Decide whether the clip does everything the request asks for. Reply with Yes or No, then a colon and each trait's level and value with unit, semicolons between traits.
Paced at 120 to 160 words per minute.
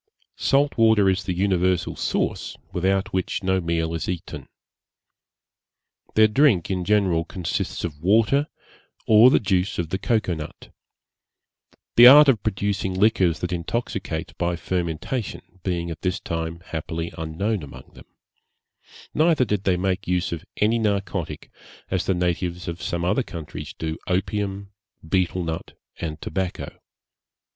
Yes: average, 140 wpm